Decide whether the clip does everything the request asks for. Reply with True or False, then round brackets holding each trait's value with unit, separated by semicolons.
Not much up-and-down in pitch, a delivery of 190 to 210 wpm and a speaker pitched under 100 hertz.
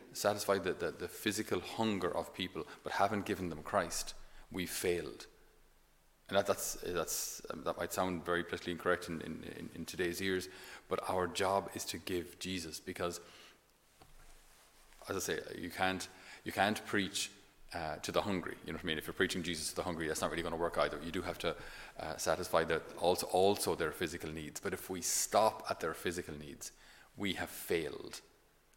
True (2.2 semitones; 195 wpm; 90 Hz)